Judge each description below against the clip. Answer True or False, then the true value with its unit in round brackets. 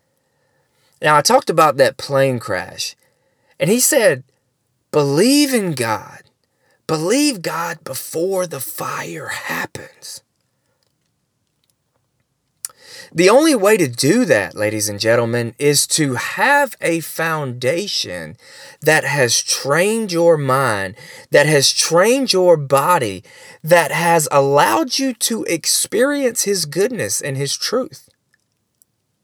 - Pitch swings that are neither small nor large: False (6.2 semitones)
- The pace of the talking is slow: True (110 wpm)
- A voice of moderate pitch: True (150 Hz)